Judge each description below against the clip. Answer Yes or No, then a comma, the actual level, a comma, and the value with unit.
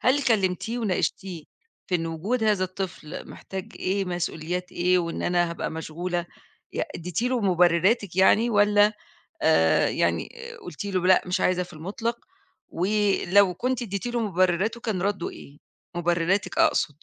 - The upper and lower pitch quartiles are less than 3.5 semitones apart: Yes, average, 3.1 semitones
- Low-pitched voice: No, medium, 185 Hz